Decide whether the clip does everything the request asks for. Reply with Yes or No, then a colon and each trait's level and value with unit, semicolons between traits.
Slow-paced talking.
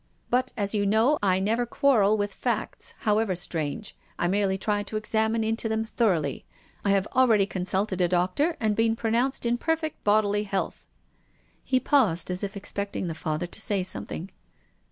No: average, 170 wpm